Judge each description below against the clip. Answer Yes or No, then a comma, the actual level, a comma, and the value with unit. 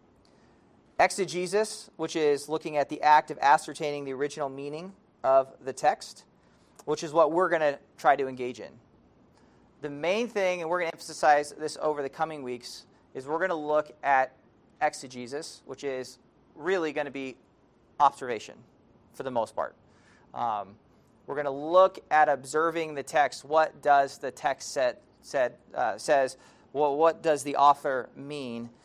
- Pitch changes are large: No, average, 2.8 semitones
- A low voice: No, medium, 150 Hz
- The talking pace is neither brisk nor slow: Yes, average, 165 wpm